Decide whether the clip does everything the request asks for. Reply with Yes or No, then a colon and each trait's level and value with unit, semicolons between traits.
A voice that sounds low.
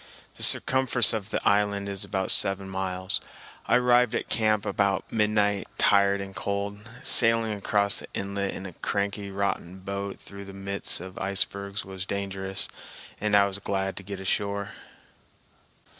Yes: low, 100 Hz